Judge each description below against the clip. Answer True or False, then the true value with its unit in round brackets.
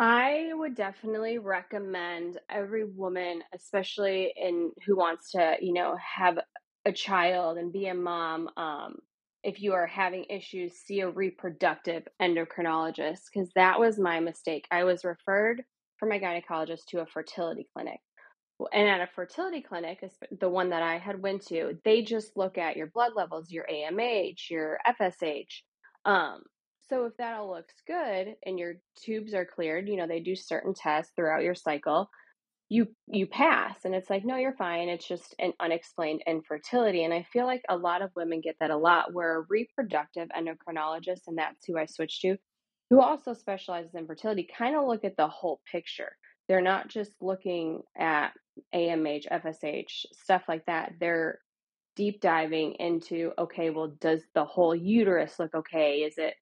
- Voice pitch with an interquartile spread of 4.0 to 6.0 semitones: False (3.4 semitones)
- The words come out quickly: False (170 wpm)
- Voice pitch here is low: False (180 Hz)